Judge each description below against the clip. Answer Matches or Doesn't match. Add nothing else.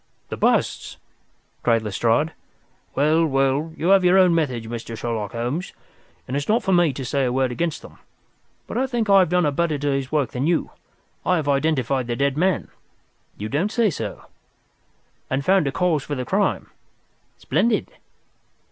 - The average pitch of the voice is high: Doesn't match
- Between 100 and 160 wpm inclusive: Doesn't match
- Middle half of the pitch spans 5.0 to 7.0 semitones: Matches